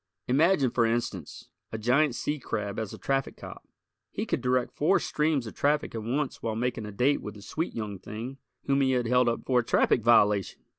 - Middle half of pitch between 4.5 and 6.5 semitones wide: No, average, 3.7 semitones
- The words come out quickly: Yes, fast, 210 wpm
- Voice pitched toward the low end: Yes, low, 125 Hz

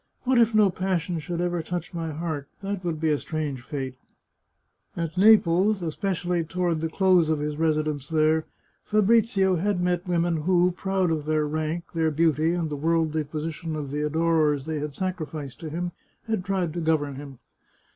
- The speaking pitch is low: No, medium, 165 Hz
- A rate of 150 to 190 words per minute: Yes, average, 180 wpm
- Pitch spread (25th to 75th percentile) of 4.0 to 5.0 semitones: No, average, 2.7 semitones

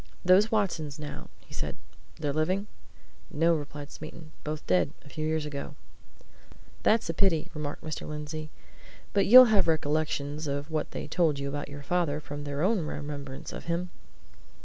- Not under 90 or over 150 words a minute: No, average, 165 wpm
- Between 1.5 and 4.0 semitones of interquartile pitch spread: Yes, narrow, 2.6 semitones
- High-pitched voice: No, medium, 155 Hz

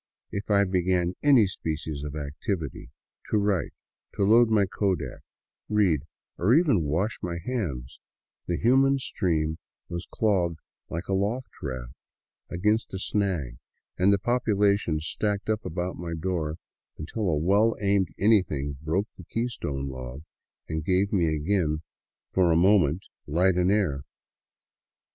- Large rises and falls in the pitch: No, average, 4.8 semitones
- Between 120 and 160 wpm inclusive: Yes, average, 140 wpm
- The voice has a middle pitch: No, very low, 90 Hz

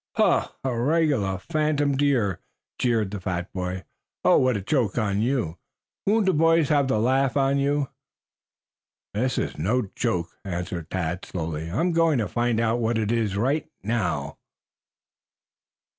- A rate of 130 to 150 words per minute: Yes, average, 145 wpm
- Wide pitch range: Yes, wide, 6.5 semitones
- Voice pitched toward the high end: No, low, 120 Hz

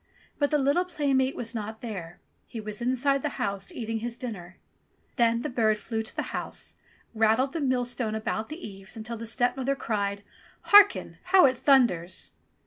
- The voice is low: No, high, 235 Hz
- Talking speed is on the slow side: No, average, 175 wpm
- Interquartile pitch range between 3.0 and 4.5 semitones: Yes, average, 3.7 semitones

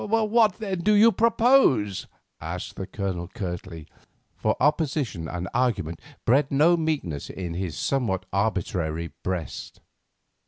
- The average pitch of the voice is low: Yes, low, 110 Hz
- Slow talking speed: Yes, slow, 120 wpm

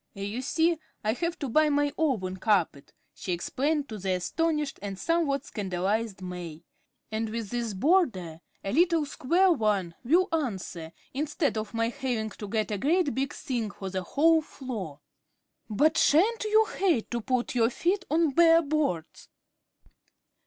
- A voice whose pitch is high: Yes, very high, 250 Hz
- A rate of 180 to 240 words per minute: No, average, 155 wpm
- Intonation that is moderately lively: No, wide, 7.8 semitones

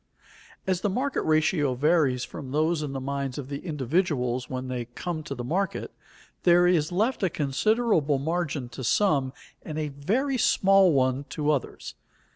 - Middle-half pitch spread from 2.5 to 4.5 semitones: No, average, 5.0 semitones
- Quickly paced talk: No, average, 165 wpm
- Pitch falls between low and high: Yes, medium, 150 Hz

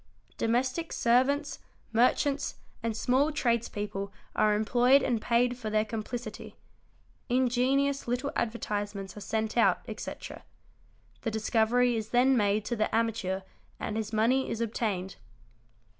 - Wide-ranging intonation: No, average, 2.7 semitones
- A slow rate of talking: Yes, slow, 125 wpm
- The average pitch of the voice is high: Yes, high, 235 Hz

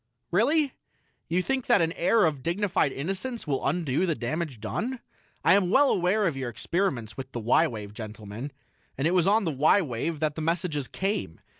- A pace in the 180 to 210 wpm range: Yes, average, 190 wpm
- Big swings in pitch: Yes, wide, 6.7 semitones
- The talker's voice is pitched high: No, medium, 165 Hz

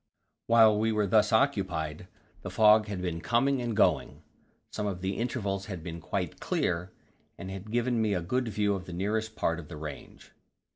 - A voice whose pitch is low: Yes, low, 105 Hz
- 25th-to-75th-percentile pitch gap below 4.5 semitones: Yes, average, 3.6 semitones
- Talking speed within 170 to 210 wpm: Yes, average, 190 wpm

